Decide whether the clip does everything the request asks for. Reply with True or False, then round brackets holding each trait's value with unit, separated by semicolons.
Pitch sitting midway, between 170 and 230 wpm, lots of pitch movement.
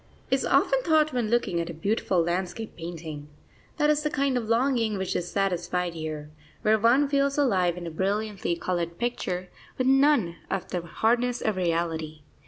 False (195 Hz; 175 wpm; 6.4 semitones)